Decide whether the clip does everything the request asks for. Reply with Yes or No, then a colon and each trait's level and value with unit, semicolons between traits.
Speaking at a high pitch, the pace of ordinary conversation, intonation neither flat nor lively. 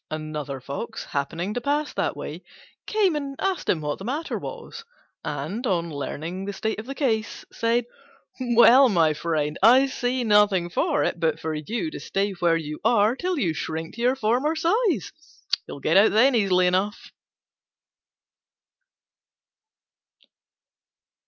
No: high, 210 Hz; average, 150 wpm; wide, 8.0 semitones